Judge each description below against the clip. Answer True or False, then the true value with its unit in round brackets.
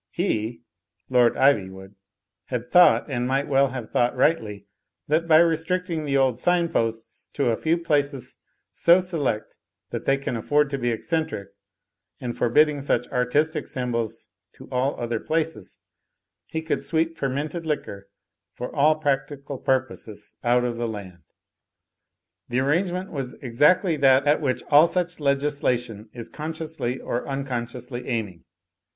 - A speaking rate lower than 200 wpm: True (145 wpm)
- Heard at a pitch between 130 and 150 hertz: True (135 Hz)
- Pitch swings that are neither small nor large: True (4.5 semitones)